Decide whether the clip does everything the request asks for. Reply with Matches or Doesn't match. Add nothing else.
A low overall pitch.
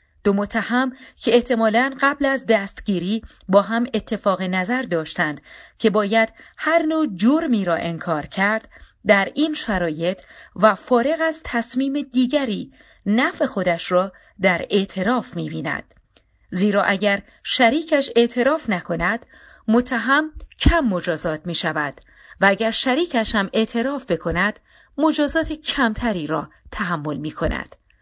Doesn't match